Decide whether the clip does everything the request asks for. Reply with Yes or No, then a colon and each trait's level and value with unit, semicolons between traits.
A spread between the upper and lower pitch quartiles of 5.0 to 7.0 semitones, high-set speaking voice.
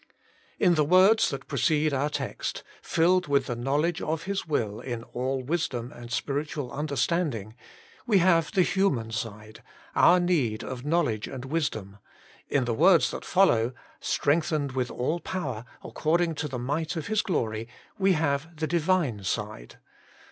No: wide, 5.6 semitones; medium, 145 Hz